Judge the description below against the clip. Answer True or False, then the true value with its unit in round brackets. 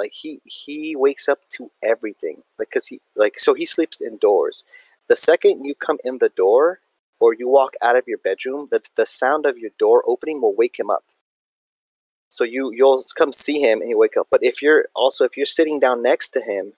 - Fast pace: True (220 wpm)